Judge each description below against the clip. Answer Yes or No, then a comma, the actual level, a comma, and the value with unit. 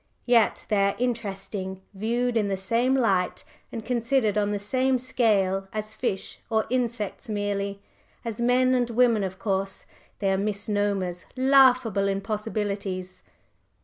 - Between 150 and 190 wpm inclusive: No, slow, 135 wpm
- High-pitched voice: Yes, high, 210 Hz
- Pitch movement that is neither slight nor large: Yes, average, 3.4 semitones